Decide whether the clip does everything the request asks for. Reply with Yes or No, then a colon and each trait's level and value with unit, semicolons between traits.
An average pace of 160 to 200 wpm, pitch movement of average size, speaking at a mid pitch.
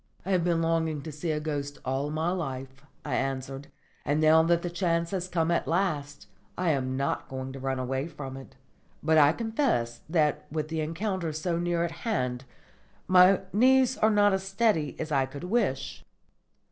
Yes: average, 185 wpm; average, 4.5 semitones; medium, 160 Hz